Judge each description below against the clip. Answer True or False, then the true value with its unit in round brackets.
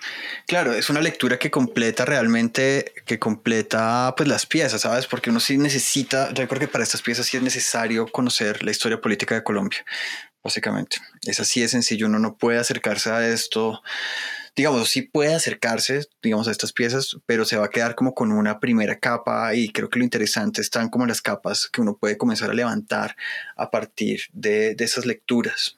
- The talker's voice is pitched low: True (125 Hz)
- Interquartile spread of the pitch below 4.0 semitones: False (4.3 semitones)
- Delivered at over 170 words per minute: True (190 wpm)